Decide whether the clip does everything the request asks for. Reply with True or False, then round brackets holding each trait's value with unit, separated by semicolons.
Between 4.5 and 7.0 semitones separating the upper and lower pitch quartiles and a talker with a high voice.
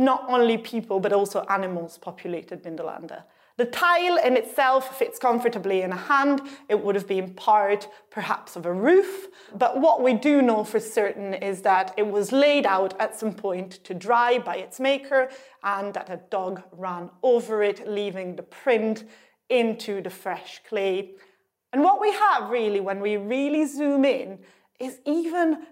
True (5.5 semitones; 220 Hz)